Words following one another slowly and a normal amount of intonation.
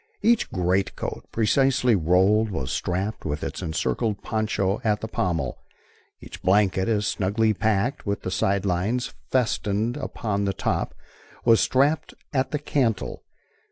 Yes: slow, 130 wpm; average, 3.6 semitones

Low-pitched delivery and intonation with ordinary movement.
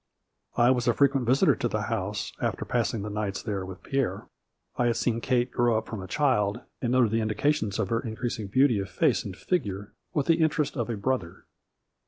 Yes: low, 120 Hz; average, 3.8 semitones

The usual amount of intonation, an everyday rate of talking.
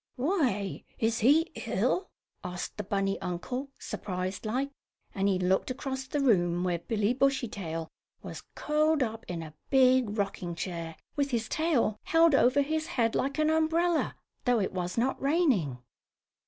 No: wide, 6.9 semitones; average, 155 wpm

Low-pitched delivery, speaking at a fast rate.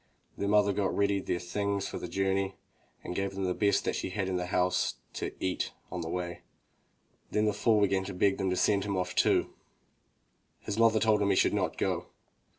Yes: low, 100 Hz; fast, 210 wpm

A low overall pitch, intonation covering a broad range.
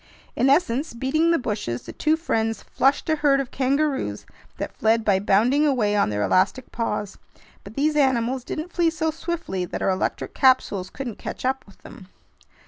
No: very high, 260 Hz; wide, 6.3 semitones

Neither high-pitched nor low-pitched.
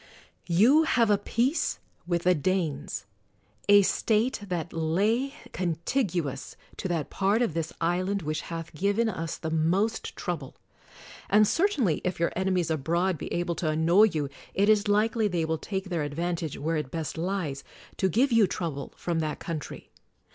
Yes: medium, 175 Hz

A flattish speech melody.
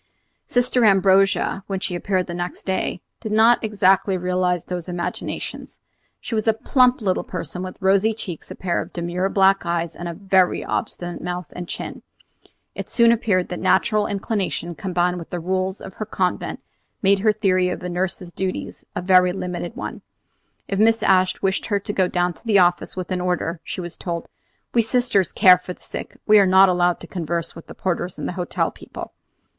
Yes: narrow, 2.0 semitones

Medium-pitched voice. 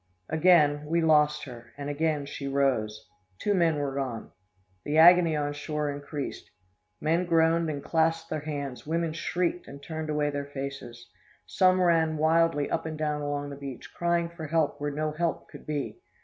Yes: medium, 150 Hz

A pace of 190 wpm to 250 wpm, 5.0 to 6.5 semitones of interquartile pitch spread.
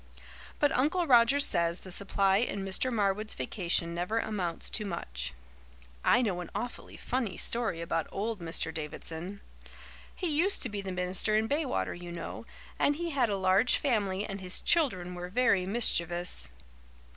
No: average, 160 wpm; average, 5.3 semitones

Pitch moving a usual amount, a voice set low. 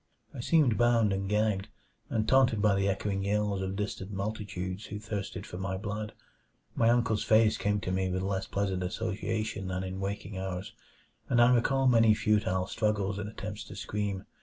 No: narrow, 2.2 semitones; low, 105 Hz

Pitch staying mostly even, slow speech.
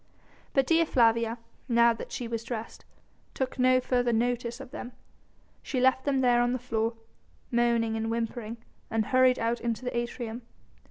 No: narrow, 1.8 semitones; average, 165 wpm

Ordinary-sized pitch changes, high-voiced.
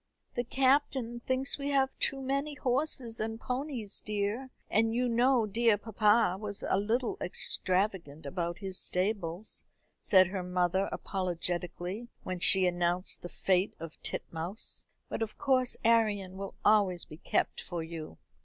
Yes: average, 4.9 semitones; high, 210 Hz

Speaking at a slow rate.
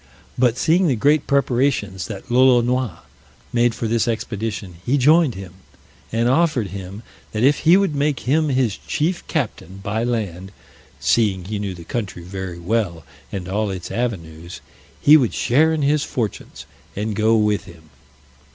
No: average, 160 wpm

